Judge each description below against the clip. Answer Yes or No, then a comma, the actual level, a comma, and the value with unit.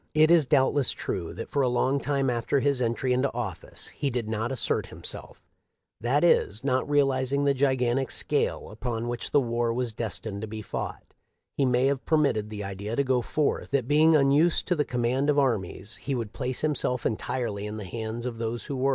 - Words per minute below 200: No, fast, 205 wpm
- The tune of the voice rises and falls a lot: No, average, 3.5 semitones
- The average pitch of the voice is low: Yes, low, 125 Hz